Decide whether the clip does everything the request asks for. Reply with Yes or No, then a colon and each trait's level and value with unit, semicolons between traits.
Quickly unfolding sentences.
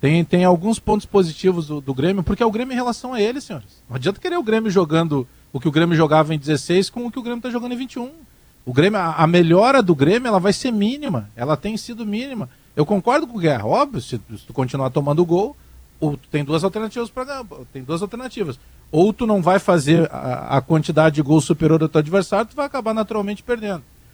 Yes: fast, 230 wpm